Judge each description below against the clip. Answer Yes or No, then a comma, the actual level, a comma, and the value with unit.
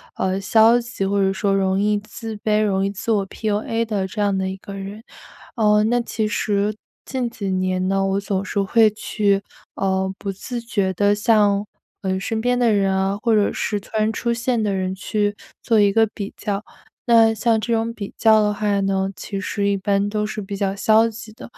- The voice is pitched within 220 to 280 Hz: No, high, 205 Hz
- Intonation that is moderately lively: No, narrow, 2.1 semitones